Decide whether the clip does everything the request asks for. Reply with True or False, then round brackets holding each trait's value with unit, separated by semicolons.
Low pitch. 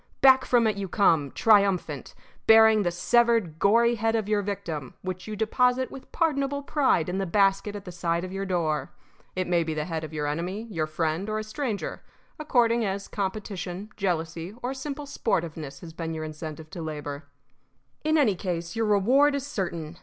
False (195 Hz)